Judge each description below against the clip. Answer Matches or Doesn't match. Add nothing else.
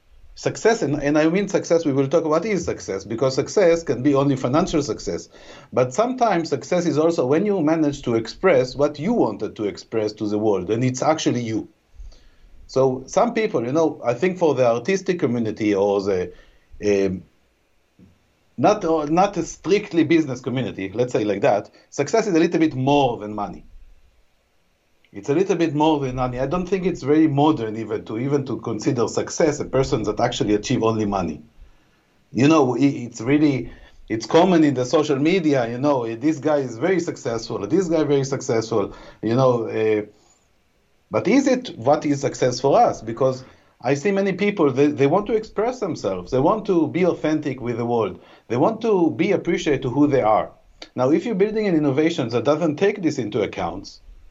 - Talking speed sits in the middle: Matches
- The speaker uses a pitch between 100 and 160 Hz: Matches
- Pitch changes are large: Matches